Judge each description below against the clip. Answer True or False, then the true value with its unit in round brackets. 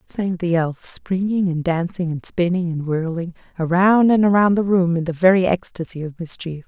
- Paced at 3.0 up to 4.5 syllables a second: False (5.0 syllables/s)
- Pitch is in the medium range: True (175 Hz)